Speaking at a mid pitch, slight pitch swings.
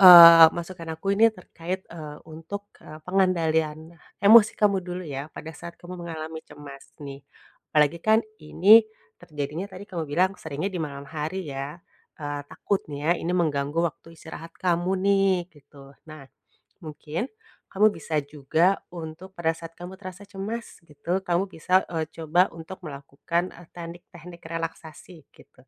No: medium, 170 Hz; average, 3.2 semitones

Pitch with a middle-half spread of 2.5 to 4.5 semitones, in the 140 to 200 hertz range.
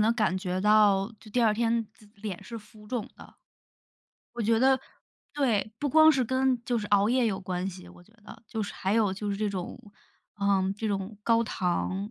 No: average, 2.8 semitones; high, 215 Hz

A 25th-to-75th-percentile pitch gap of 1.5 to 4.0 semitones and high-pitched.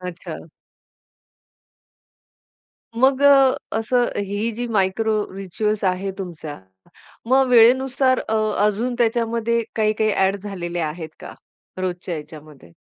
No: average, 4.7 semitones; high, 215 Hz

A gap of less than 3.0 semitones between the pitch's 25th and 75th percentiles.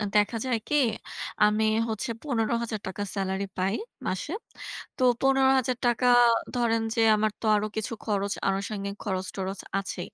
No: average, 3.3 semitones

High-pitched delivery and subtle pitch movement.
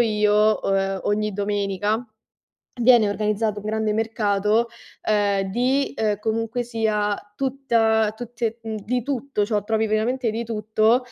Yes: high, 220 Hz; narrow, 2.0 semitones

